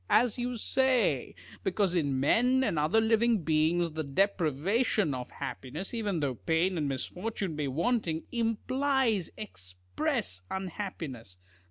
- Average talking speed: No, slow, 125 wpm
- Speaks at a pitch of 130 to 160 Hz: No, medium, 180 Hz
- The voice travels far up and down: Yes, wide, 7.5 semitones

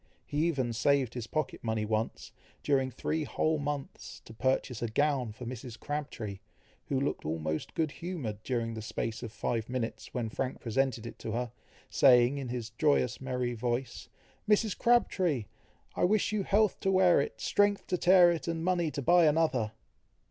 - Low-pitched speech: Yes, low, 130 Hz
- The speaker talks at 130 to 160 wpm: No, average, 175 wpm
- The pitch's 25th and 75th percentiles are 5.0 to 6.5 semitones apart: Yes, wide, 5.6 semitones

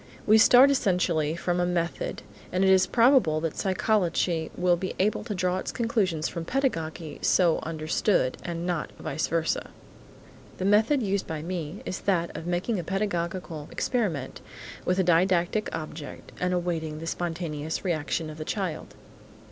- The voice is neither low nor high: Yes, medium, 175 Hz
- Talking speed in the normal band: Yes, average, 155 wpm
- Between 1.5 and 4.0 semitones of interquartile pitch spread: Yes, average, 3.0 semitones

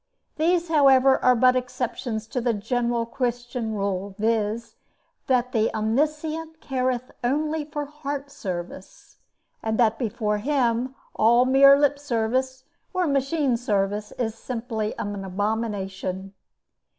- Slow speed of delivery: Yes, slow, 120 wpm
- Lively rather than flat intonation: No, average, 3.9 semitones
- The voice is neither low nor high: No, high, 245 Hz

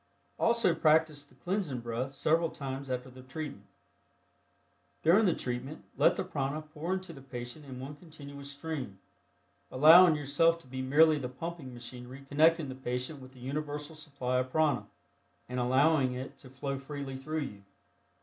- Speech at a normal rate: Yes, average, 160 wpm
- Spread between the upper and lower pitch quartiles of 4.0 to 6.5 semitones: No, average, 3.4 semitones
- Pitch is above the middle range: No, medium, 140 Hz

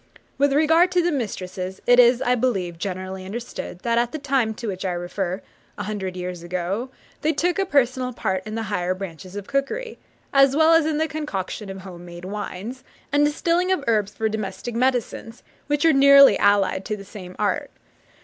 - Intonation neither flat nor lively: No, wide, 6.8 semitones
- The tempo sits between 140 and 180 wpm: No, average, 195 wpm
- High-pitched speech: Yes, high, 225 Hz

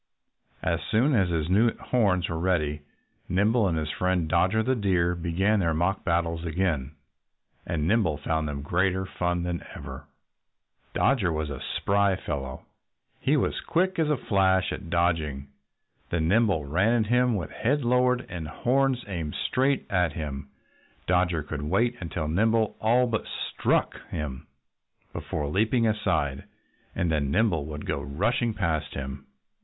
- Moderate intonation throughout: No, wide, 5.9 semitones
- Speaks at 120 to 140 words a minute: No, average, 150 wpm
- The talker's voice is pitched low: Yes, very low, 90 Hz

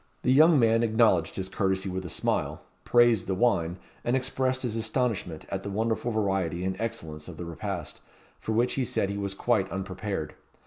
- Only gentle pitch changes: No, average, 3.9 semitones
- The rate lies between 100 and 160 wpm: No, average, 185 wpm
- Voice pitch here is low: Yes, low, 100 Hz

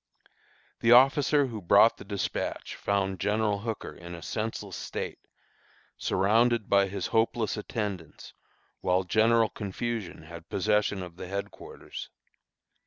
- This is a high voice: No, low, 105 Hz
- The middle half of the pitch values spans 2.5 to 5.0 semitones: Yes, average, 3.1 semitones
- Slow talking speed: Yes, slow, 120 wpm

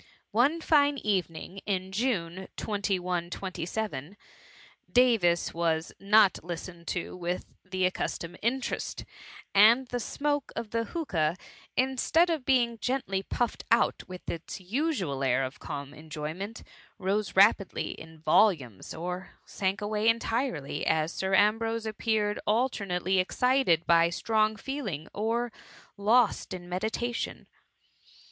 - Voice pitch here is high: Yes, high, 200 Hz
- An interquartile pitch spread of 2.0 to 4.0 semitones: No, average, 5.1 semitones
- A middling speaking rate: No, slow, 130 wpm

